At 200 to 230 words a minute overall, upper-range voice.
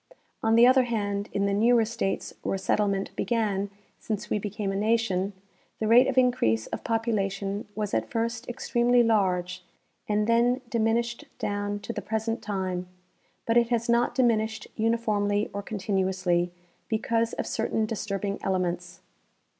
No: average, 150 wpm; high, 215 Hz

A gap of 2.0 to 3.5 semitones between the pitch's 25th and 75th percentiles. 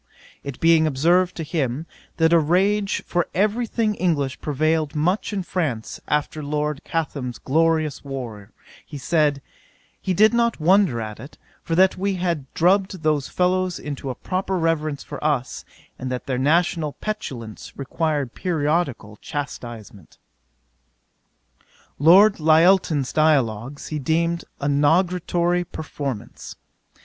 No: average, 4.2 semitones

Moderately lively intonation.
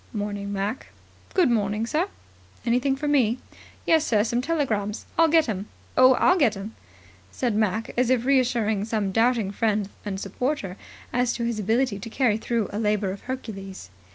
Yes: average, 3.8 semitones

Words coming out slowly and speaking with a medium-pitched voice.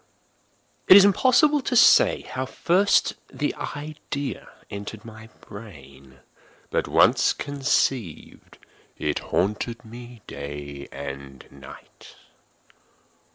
No: slow, 95 wpm; low, 110 Hz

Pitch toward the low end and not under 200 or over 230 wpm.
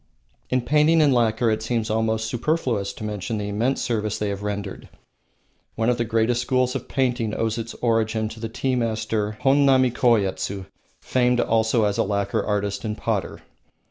No: low, 115 Hz; average, 175 wpm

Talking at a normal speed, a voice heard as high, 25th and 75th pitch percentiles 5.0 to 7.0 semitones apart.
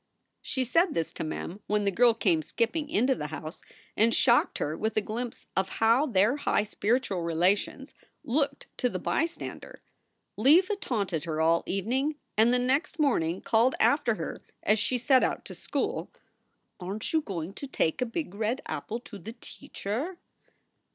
Yes: average, 170 wpm; high, 225 Hz; wide, 5.5 semitones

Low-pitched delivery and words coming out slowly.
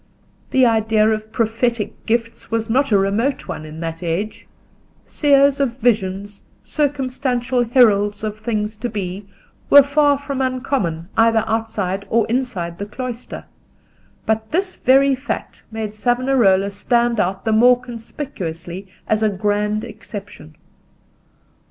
No: high, 225 Hz; slow, 130 wpm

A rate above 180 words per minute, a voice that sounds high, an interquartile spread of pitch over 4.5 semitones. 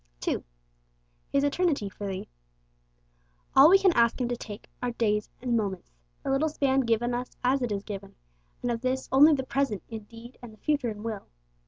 No: average, 195 wpm; high, 240 Hz; average, 4.0 semitones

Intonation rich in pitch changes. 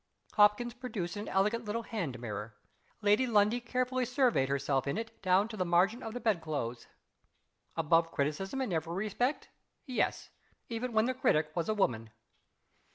Yes: wide, 6.6 semitones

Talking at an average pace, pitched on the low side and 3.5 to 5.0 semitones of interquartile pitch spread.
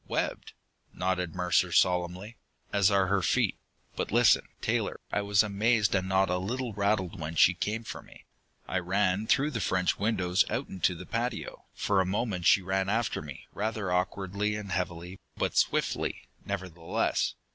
No: average, 165 wpm; very low, 95 Hz; average, 2.7 semitones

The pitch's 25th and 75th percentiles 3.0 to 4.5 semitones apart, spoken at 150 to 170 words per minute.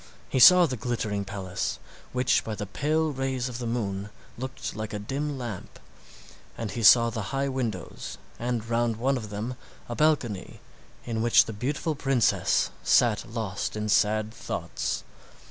Yes: average, 3.6 semitones; average, 160 wpm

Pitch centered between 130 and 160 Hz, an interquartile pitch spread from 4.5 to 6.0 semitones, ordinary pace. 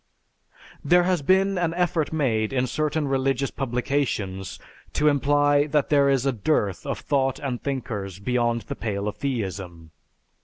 Yes: low, 135 Hz; average, 4.8 semitones; average, 150 wpm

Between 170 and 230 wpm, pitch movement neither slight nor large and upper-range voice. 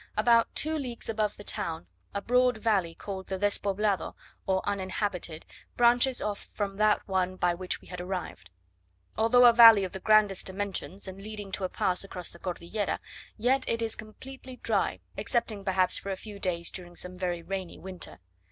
Yes: average, 180 wpm; average, 3.0 semitones; high, 200 Hz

